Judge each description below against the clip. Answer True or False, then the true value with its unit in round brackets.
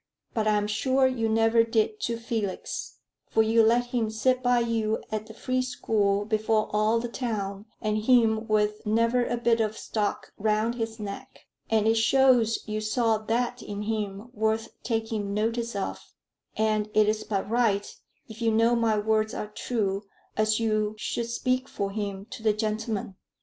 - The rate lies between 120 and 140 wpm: False (170 wpm)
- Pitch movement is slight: True (1.5 semitones)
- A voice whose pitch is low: False (220 Hz)